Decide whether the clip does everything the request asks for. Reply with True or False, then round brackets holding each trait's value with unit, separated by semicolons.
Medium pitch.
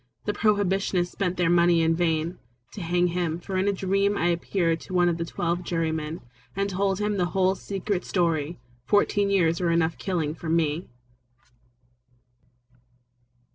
True (175 Hz)